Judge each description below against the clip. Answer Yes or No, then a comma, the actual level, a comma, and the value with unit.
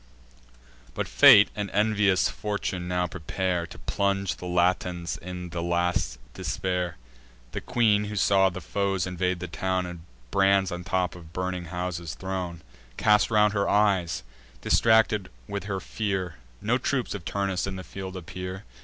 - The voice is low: Yes, very low, 95 Hz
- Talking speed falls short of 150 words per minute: No, average, 155 wpm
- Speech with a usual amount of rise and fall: No, narrow, 2.2 semitones